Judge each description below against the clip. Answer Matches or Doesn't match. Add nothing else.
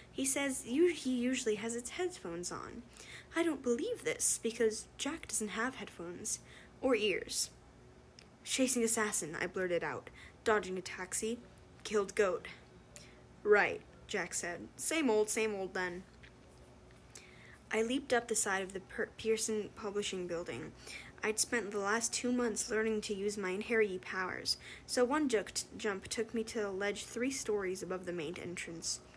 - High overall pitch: Matches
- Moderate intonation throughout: Matches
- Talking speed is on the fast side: Doesn't match